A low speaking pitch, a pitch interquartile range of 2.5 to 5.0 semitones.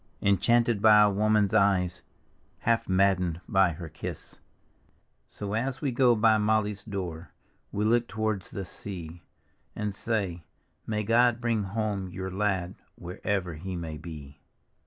Yes: low, 100 Hz; average, 3.2 semitones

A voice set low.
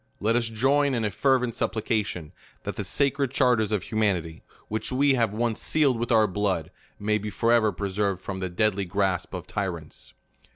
Yes: low, 110 Hz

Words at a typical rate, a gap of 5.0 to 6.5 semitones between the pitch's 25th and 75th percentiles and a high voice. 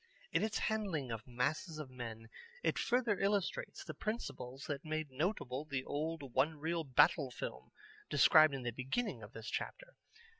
No: average, 160 wpm; wide, 5.4 semitones; medium, 150 Hz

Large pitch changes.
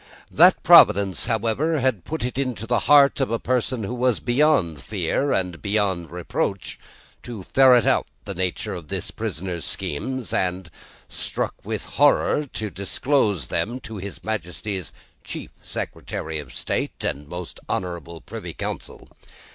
Yes: wide, 6.0 semitones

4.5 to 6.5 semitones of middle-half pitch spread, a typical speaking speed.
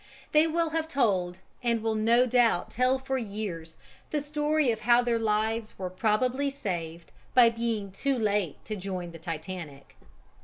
Yes: average, 5.3 semitones; average, 160 wpm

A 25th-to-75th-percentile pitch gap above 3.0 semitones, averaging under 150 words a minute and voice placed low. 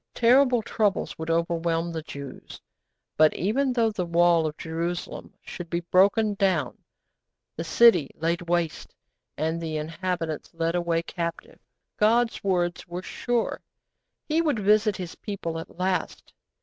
No: average, 4.0 semitones; slow, 135 wpm; medium, 175 Hz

